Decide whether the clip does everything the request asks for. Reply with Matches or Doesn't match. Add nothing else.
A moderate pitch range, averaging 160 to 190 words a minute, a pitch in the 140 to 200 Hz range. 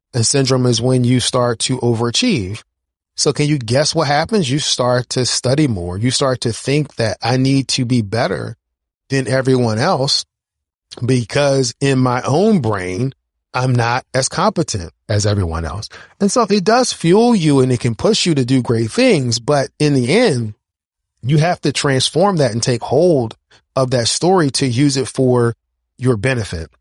Doesn't match